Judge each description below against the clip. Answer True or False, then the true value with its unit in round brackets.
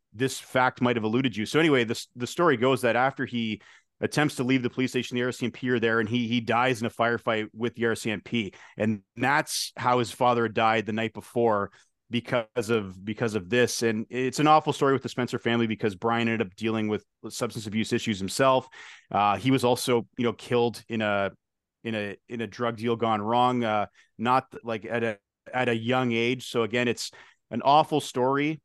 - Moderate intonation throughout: False (2.0 semitones)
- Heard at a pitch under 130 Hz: True (120 Hz)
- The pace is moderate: False (210 wpm)